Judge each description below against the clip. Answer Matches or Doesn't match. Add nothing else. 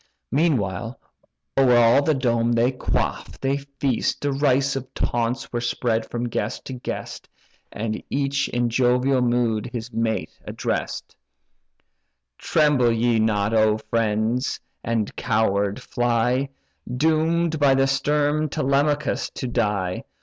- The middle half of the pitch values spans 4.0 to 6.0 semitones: Doesn't match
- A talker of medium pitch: Doesn't match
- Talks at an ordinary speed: Doesn't match